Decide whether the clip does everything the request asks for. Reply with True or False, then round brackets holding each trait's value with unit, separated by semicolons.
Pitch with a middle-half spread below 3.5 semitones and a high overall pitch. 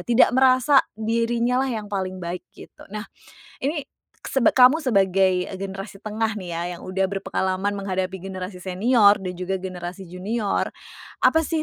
False (4.1 semitones; 200 Hz)